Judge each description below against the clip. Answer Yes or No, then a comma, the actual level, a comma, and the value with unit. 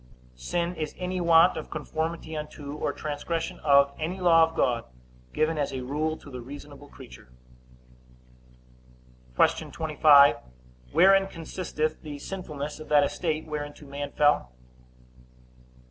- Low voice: No, medium, 150 Hz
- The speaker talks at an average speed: No, slow, 130 wpm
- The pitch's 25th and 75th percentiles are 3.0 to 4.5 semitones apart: No, narrow, 2.4 semitones